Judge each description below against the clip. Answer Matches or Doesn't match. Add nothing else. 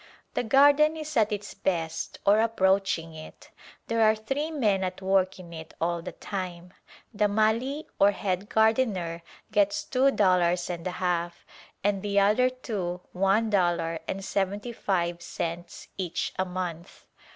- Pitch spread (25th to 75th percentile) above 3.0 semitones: Matches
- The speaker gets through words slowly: Doesn't match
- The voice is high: Matches